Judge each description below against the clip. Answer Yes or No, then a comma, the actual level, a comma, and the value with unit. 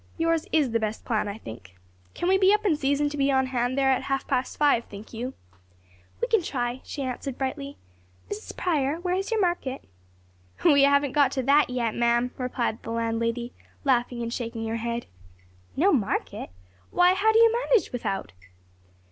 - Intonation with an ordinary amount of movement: Yes, average, 4.9 semitones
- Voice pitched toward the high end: Yes, very high, 265 Hz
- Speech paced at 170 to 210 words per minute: Yes, average, 185 wpm